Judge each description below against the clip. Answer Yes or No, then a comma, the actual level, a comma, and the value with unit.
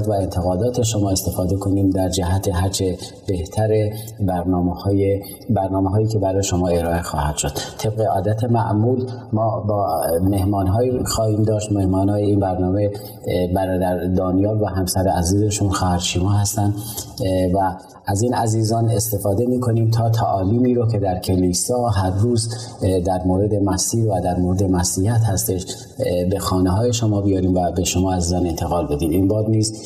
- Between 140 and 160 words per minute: Yes, average, 150 wpm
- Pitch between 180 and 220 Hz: No, low, 100 Hz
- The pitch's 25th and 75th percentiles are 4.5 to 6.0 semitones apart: No, average, 2.7 semitones